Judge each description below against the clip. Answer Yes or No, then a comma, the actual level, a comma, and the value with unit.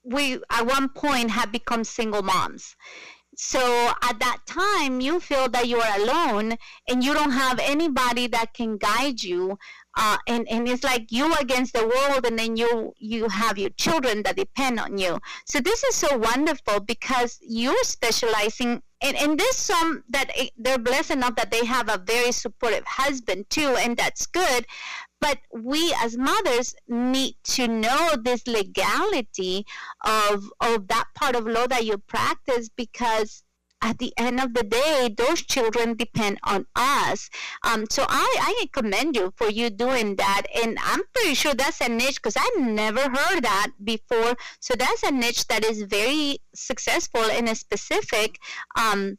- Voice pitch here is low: No, high, 240 Hz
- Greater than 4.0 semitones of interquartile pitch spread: No, average, 3.1 semitones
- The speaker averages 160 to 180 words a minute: Yes, average, 170 wpm